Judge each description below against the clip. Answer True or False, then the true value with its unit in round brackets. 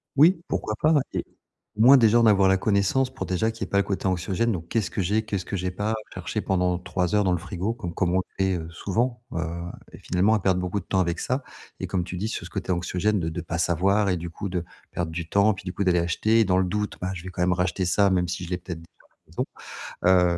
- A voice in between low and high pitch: False (95 Hz)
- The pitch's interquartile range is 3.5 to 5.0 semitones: False (2.9 semitones)